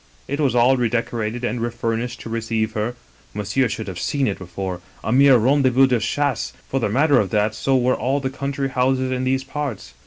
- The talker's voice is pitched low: Yes, low, 125 Hz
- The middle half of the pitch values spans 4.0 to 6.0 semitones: No, average, 3.4 semitones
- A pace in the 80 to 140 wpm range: No, fast, 205 wpm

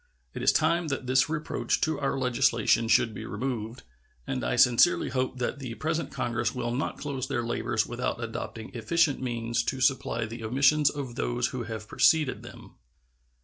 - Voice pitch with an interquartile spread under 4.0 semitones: Yes, average, 3.0 semitones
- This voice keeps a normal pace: Yes, average, 175 wpm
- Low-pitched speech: Yes, low, 125 Hz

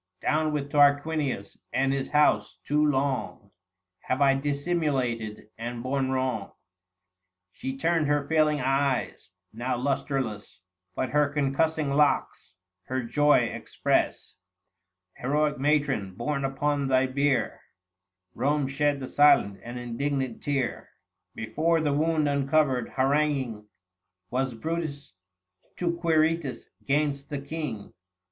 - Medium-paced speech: No, slow, 115 wpm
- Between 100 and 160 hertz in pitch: Yes, medium, 140 Hz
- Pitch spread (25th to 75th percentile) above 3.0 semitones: No, narrow, 2.6 semitones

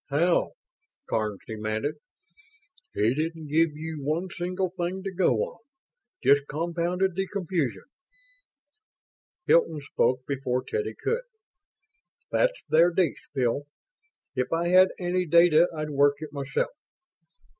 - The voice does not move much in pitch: No, average, 4.1 semitones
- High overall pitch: No, medium, 160 Hz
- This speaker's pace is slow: Yes, slow, 120 wpm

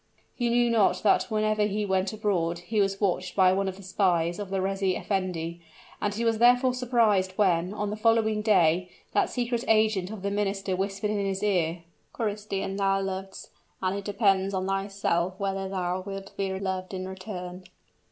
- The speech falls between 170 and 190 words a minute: Yes, average, 180 wpm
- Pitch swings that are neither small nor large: No, narrow, 2.1 semitones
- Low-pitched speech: No, high, 195 Hz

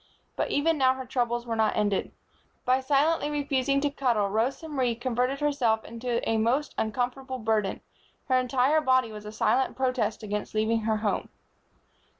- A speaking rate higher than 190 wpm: No, average, 160 wpm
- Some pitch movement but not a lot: Yes, average, 3.4 semitones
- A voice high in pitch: Yes, very high, 250 Hz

